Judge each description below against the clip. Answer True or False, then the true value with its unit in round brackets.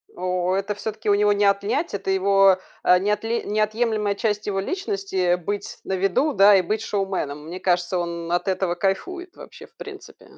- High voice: True (195 Hz)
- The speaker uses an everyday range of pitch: False (2.2 semitones)